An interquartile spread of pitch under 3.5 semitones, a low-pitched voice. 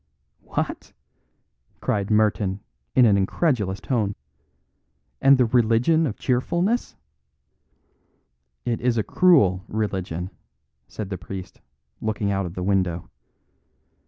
No: average, 4.5 semitones; low, 105 Hz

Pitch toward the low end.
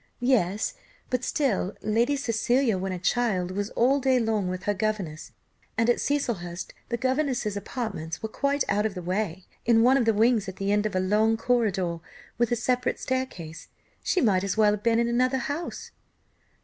No: high, 220 Hz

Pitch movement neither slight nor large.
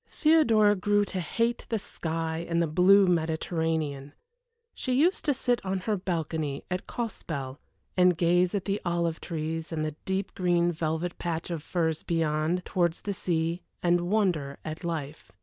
Yes: average, 3.0 semitones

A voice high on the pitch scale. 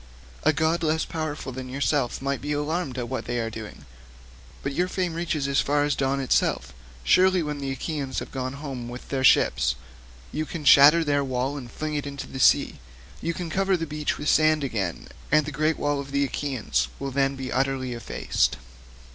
No: medium, 140 Hz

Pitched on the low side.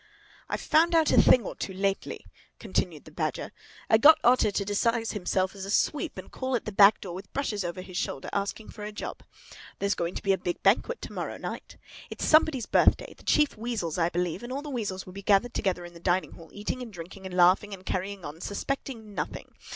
No: high, 200 Hz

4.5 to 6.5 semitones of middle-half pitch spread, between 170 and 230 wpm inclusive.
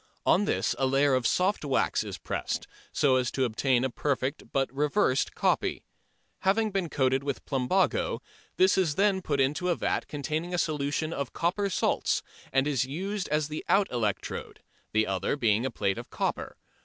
Yes: average, 5.3 semitones; average, 180 wpm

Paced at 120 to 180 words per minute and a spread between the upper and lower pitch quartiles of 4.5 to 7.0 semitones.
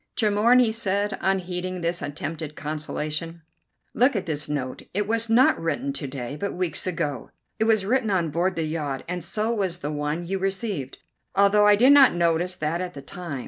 No: average, 190 wpm; average, 5.2 semitones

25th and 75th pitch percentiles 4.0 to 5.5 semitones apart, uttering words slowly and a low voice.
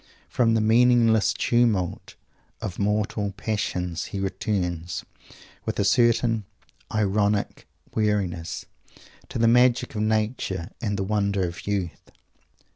No: average, 2.8 semitones; slow, 115 wpm; low, 105 Hz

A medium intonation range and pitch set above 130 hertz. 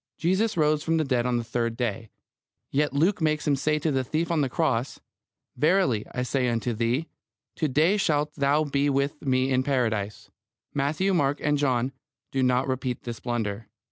Yes: average, 3.8 semitones; medium, 140 Hz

